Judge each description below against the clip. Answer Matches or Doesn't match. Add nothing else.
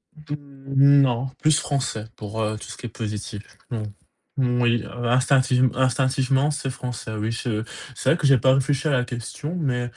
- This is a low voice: Matches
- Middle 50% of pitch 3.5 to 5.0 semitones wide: Doesn't match